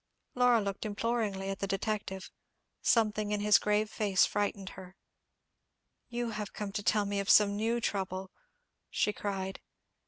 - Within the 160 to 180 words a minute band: No, average, 150 wpm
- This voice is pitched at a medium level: No, high, 205 Hz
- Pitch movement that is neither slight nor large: No, narrow, 1.7 semitones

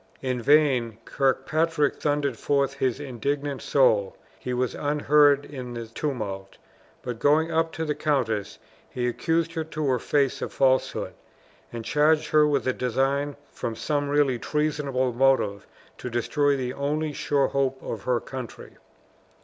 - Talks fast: No, average, 150 wpm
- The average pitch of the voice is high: No, medium, 140 Hz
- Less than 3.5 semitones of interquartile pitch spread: Yes, average, 2.9 semitones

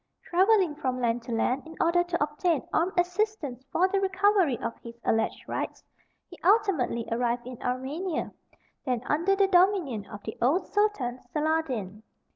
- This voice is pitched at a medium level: No, very high, 310 Hz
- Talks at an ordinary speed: Yes, average, 155 wpm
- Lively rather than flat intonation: Yes, wide, 7.2 semitones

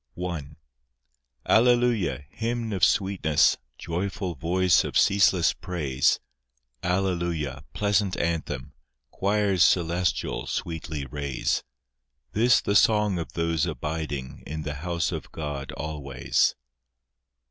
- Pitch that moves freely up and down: No, average, 4.5 semitones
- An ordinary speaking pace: No, slow, 100 wpm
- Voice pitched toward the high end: No, very low, 85 Hz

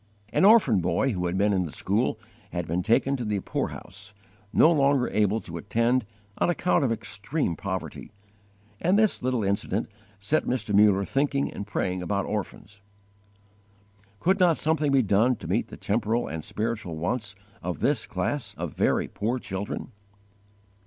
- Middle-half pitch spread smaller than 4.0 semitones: No, average, 5.1 semitones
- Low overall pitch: Yes, low, 110 Hz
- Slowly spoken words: No, average, 165 wpm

